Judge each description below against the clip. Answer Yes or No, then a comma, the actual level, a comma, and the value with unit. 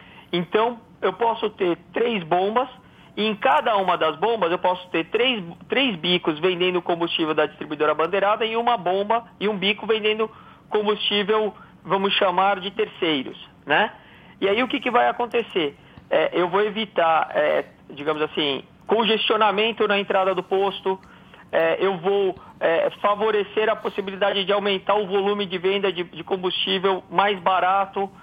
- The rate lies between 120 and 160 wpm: Yes, average, 155 wpm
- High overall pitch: Yes, high, 200 Hz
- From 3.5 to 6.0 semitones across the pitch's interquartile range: No, average, 2.9 semitones